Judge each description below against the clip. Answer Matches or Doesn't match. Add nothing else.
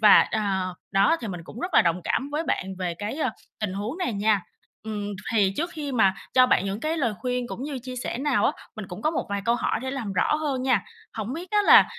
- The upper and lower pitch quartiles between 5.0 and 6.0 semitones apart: Matches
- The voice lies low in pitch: Doesn't match